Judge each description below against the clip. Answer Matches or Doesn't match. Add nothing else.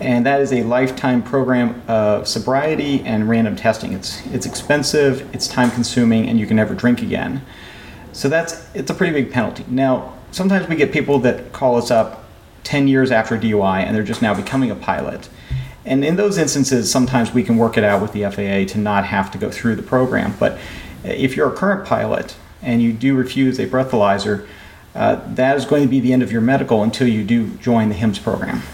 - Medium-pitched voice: Doesn't match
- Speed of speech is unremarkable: Doesn't match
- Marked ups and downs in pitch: Doesn't match